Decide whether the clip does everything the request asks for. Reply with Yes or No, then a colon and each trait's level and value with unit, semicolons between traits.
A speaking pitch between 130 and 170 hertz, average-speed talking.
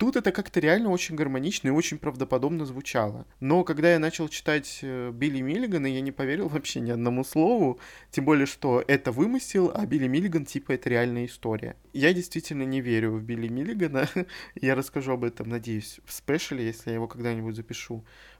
No: low, 135 Hz; fast, 180 wpm